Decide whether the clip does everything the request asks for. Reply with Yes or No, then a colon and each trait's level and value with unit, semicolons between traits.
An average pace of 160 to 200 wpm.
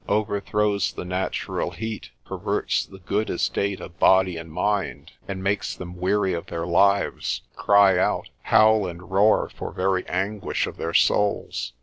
No: average, 150 wpm